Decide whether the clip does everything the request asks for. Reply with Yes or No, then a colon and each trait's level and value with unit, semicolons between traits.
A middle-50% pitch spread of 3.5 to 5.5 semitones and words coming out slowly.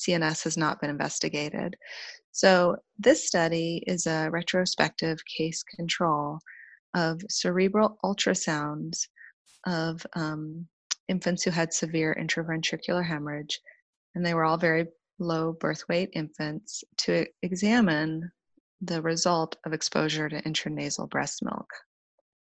No: narrow, 2.6 semitones; slow, 115 wpm